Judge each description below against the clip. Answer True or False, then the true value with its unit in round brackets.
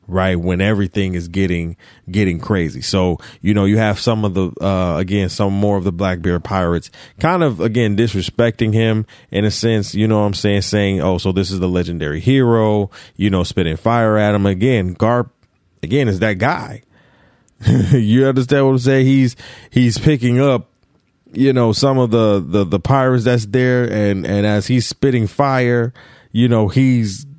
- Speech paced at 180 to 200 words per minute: True (185 wpm)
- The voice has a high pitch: False (105 Hz)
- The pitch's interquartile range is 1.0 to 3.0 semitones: False (4.2 semitones)